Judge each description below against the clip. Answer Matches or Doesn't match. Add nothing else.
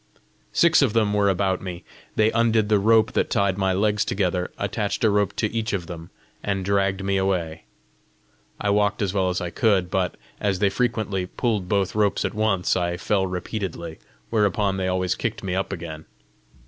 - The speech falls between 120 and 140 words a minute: Doesn't match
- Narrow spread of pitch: Matches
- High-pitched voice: Doesn't match